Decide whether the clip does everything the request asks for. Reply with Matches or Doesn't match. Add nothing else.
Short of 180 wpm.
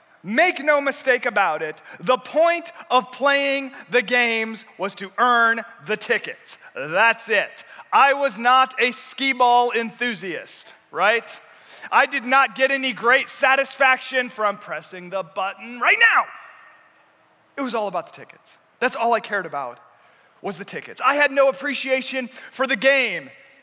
Matches